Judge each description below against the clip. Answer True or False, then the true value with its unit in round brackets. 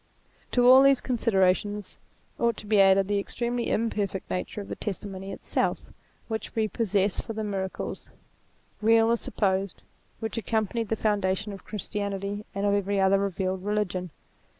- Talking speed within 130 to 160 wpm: True (150 wpm)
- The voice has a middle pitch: False (205 Hz)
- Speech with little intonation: True (2.3 semitones)